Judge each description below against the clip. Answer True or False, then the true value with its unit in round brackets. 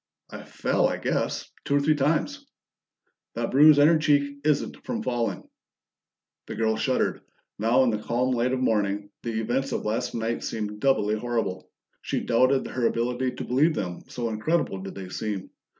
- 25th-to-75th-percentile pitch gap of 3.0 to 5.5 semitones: True (4.5 semitones)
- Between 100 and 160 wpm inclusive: False (175 wpm)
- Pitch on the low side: True (120 Hz)